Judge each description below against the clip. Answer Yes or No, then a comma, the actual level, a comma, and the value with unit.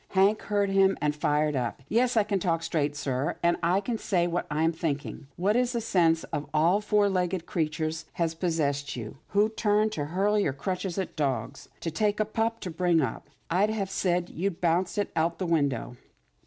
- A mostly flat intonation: No, average, 4.5 semitones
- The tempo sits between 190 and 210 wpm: Yes, fast, 205 wpm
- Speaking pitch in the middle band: Yes, medium, 175 Hz